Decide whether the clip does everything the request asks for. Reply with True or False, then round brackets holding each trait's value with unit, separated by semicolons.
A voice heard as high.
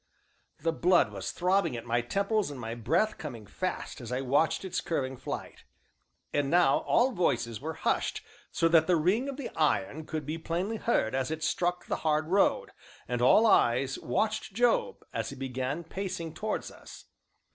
False (160 Hz)